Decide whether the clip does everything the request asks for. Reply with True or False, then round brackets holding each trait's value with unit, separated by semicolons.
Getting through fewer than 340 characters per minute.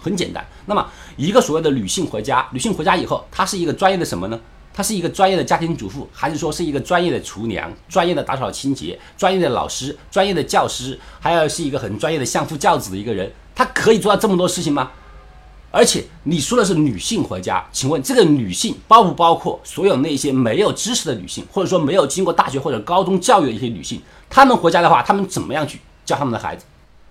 False (370 characters per minute)